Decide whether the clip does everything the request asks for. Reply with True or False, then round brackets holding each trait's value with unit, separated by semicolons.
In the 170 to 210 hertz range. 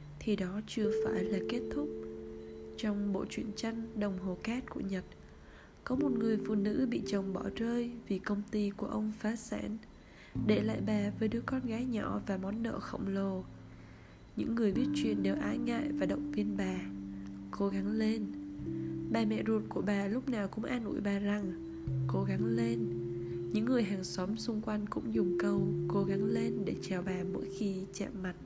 True (185 Hz)